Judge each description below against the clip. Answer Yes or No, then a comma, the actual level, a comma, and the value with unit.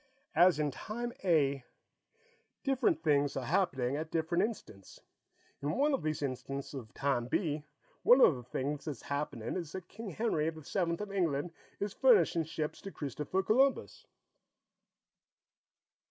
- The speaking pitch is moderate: Yes, medium, 155 Hz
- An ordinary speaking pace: Yes, average, 145 wpm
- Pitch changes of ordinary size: No, wide, 5.7 semitones